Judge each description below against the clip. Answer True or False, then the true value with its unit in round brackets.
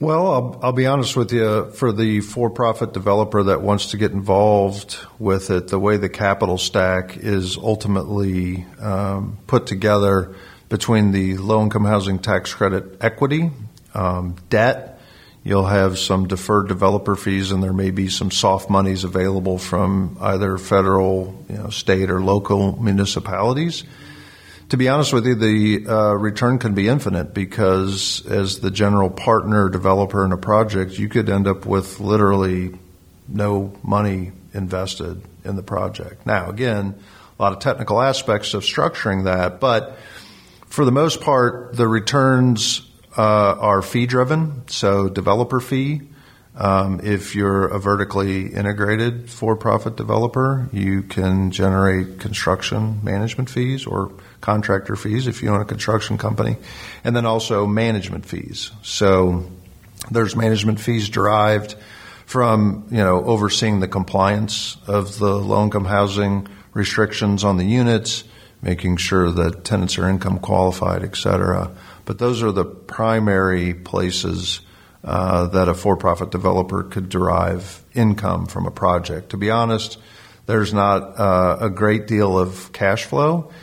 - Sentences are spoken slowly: False (145 wpm)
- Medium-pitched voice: False (100 Hz)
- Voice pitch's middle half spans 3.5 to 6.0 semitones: False (2.6 semitones)